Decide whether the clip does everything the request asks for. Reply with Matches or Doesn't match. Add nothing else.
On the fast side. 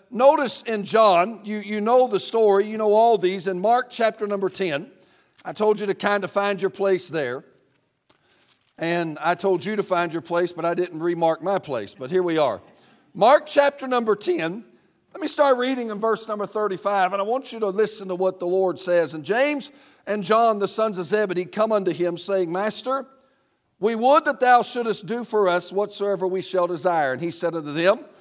Matches